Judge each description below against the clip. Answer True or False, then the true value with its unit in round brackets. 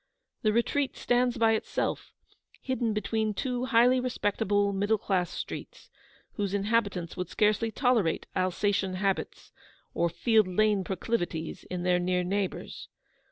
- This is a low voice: False (205 Hz)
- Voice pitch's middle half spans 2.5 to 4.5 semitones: True (3.8 semitones)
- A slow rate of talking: True (125 wpm)